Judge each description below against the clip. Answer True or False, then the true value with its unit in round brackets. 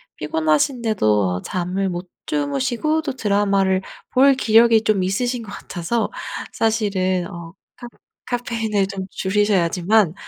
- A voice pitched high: True (200 Hz)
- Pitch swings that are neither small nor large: True (4.3 semitones)